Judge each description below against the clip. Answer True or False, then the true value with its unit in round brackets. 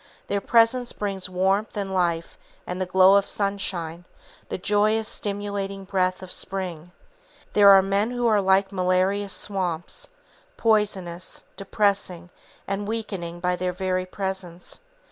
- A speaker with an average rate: False (130 wpm)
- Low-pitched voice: False (195 Hz)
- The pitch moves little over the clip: True (1.9 semitones)